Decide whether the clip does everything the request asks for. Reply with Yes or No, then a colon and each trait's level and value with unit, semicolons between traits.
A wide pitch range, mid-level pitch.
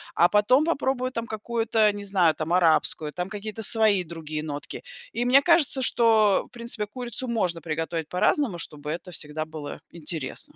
No: wide, 6.3 semitones; high, 205 Hz